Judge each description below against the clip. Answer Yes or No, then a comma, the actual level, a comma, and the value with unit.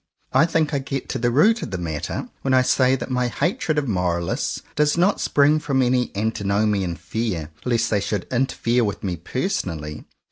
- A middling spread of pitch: No, wide, 6.1 semitones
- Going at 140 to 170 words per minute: No, average, 185 wpm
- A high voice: No, low, 120 Hz